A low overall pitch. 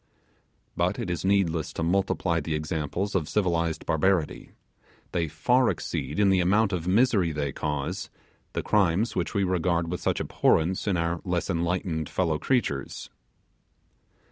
Yes: very low, 85 Hz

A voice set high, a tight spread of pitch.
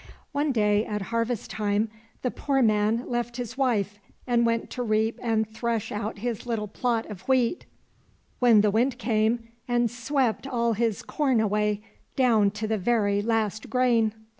Yes: high, 230 Hz; narrow, 2.3 semitones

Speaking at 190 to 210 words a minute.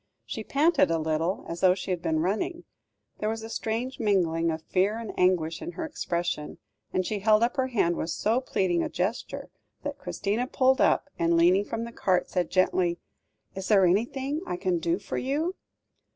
Yes: average, 195 wpm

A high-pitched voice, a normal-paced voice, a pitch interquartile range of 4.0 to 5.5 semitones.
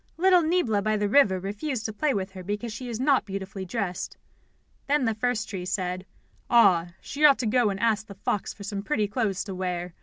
No: high, 210 Hz; fast, 215 wpm; average, 4.4 semitones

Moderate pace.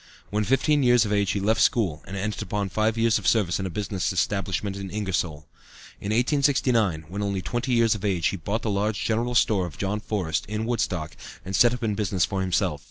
No: fast, 220 wpm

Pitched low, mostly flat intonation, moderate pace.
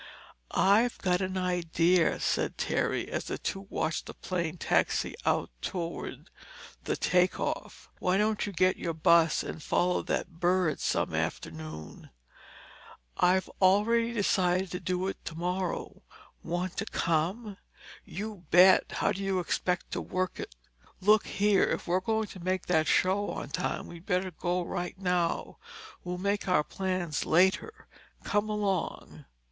No: medium, 185 Hz; narrow, 2.0 semitones; average, 145 wpm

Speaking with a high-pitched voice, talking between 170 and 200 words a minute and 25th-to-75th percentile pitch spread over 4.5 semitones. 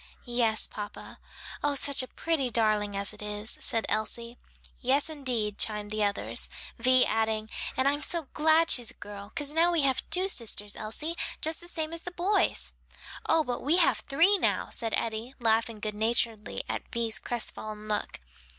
Yes: high, 235 Hz; average, 180 wpm; wide, 5.6 semitones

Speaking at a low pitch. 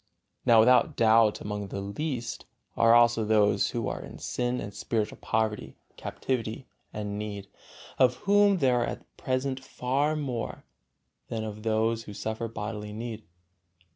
Yes: low, 115 Hz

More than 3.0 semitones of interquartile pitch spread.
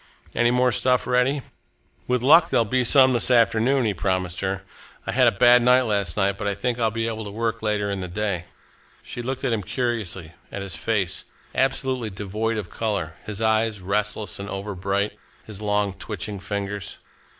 Yes: average, 3.4 semitones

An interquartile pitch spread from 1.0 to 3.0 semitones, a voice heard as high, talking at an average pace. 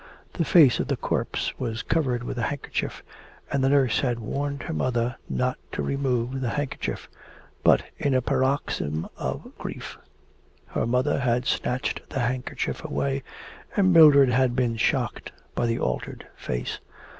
No: average, 2.7 semitones; low, 130 Hz; average, 155 wpm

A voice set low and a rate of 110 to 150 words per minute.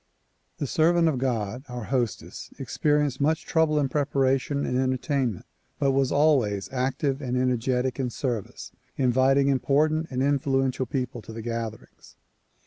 Yes: low, 130 Hz; average, 140 wpm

